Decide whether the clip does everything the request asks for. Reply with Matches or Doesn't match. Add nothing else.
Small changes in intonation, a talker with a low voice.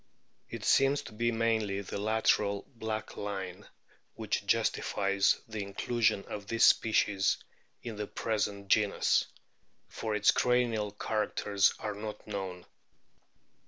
Matches